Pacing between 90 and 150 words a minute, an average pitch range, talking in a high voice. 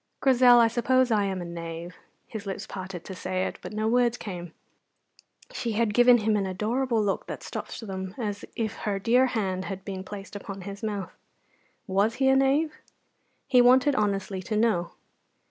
No: average, 180 wpm; average, 4.1 semitones; high, 210 Hz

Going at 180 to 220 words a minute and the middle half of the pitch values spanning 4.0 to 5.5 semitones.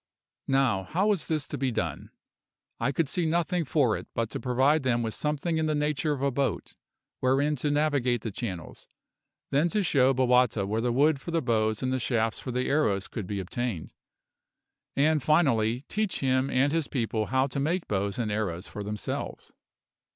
Yes: average, 190 wpm; average, 4.8 semitones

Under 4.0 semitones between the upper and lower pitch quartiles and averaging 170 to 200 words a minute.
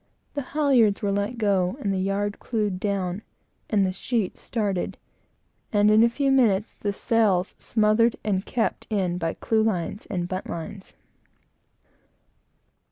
No: average, 3.0 semitones; slow, 135 wpm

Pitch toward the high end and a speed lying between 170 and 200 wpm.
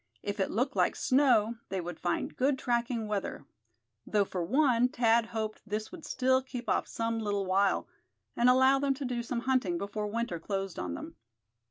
Yes: high, 230 Hz; average, 185 wpm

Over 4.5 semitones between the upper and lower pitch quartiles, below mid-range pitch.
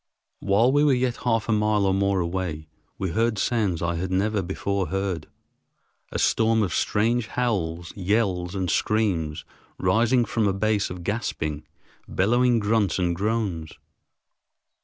No: average, 4.0 semitones; low, 100 Hz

